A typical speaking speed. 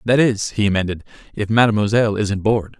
Yes: average, 170 wpm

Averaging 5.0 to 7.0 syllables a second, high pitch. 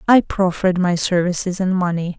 No: 5.4 syllables/s; medium, 180 Hz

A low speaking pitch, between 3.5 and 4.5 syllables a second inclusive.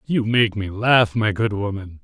Yes: low, 105 Hz; 4.2 syllables/s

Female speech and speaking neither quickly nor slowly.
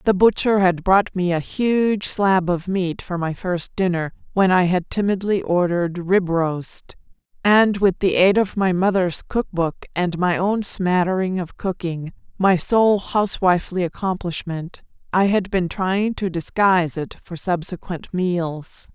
Yes: female; average, 160 wpm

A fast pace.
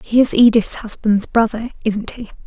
No: average, 170 wpm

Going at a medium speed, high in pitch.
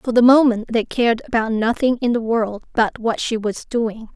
No: fast, 215 wpm; high, 230 Hz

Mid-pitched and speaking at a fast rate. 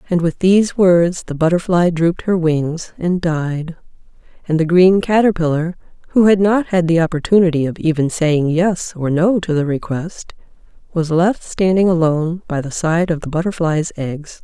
No: medium, 170 Hz; average, 170 wpm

